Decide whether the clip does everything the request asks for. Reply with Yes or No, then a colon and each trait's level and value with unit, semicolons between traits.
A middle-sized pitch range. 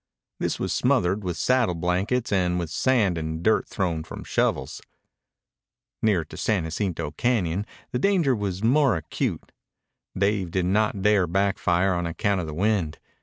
Yes: average, 3.7 semitones